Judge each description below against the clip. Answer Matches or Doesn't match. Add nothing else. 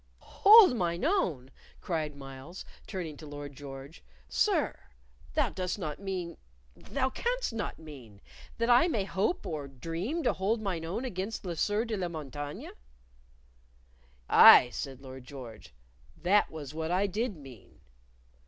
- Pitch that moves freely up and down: Matches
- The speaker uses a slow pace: Doesn't match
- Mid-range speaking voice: Matches